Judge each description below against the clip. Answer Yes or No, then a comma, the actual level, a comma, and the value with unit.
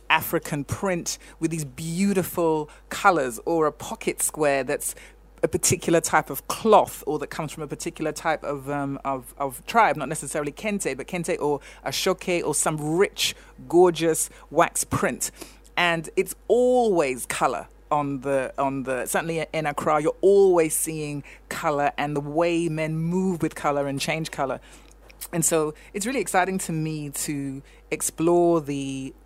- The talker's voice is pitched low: No, medium, 160 Hz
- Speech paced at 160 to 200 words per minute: No, average, 150 wpm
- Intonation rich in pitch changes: No, average, 3.1 semitones